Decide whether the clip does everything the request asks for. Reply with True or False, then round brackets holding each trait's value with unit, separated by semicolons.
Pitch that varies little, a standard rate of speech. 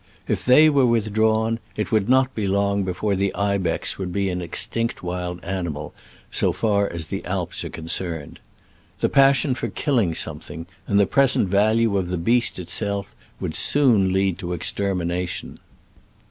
False (3.9 semitones; 160 wpm)